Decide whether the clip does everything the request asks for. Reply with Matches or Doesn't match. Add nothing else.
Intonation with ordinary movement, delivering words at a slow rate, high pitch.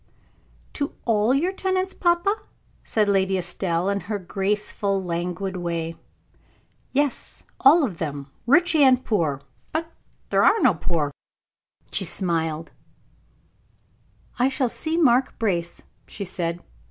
Doesn't match